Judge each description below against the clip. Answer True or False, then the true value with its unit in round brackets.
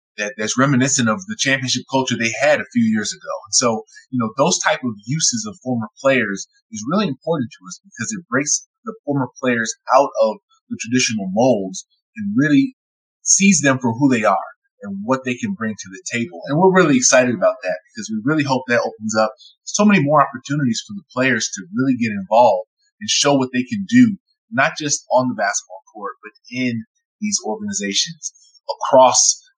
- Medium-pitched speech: True (145 Hz)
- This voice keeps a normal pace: True (195 wpm)